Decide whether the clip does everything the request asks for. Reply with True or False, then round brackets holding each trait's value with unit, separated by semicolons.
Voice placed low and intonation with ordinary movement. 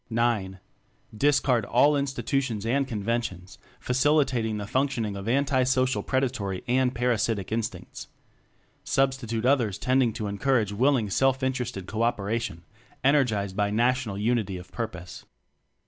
True (120 Hz; 4.1 semitones)